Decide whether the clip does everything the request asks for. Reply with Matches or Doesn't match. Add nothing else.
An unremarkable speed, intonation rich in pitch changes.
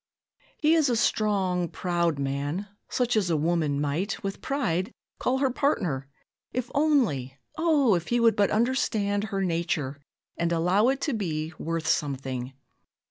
Matches